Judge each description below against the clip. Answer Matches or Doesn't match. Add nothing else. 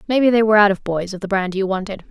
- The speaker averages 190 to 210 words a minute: Doesn't match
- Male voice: Doesn't match